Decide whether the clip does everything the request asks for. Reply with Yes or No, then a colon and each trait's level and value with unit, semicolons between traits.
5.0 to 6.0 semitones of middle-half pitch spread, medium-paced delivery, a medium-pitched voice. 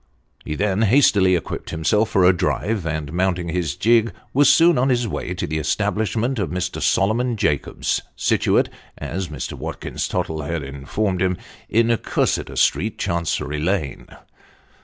No: wide, 5.4 semitones; average, 150 wpm; very low, 95 Hz